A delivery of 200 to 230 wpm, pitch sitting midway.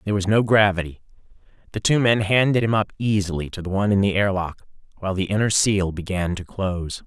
No: fast, 205 wpm; low, 100 Hz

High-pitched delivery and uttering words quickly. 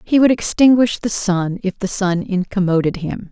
No: high, 195 Hz; average, 180 wpm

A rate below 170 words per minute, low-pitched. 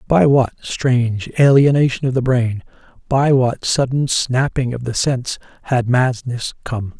Yes: average, 145 wpm; low, 130 Hz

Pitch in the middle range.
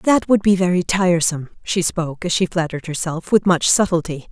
Yes: medium, 175 Hz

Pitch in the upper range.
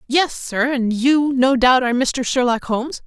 Yes: very high, 255 Hz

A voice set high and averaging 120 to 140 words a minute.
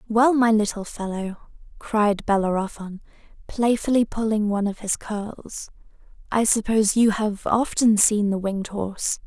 Yes: high, 210 Hz; slow, 135 wpm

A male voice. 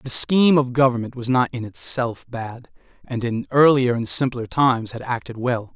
Yes: male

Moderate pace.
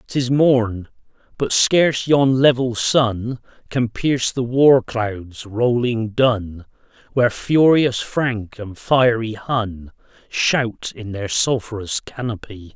No: slow, 120 wpm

